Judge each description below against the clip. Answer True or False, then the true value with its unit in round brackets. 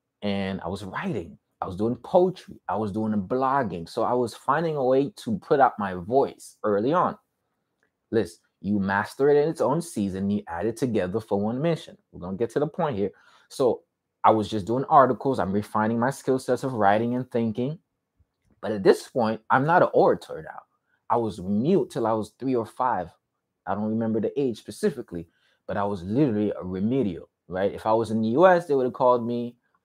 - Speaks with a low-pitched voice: True (115 Hz)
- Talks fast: True (210 wpm)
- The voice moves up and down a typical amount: True (4.7 semitones)